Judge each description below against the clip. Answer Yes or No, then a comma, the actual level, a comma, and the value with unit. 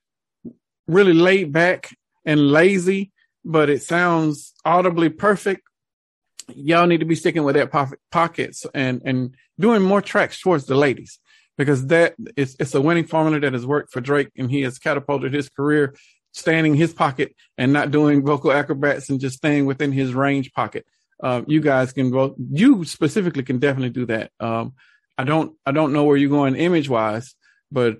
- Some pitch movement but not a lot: Yes, average, 3.6 semitones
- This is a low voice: No, medium, 145 Hz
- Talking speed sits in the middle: Yes, average, 180 wpm